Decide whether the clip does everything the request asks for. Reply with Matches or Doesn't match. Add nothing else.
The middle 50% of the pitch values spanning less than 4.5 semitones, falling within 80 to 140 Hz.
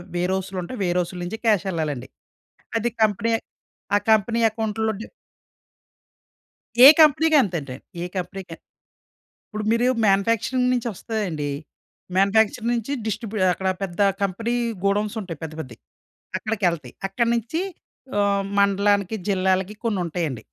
Doesn't match